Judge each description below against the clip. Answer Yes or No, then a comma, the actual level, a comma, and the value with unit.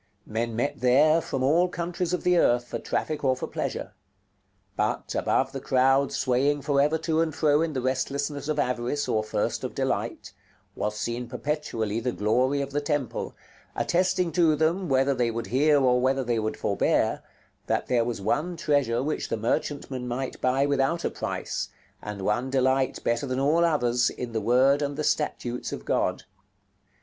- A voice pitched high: No, low, 135 Hz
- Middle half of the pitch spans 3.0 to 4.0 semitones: Yes, average, 3.6 semitones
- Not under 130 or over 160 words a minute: No, average, 180 wpm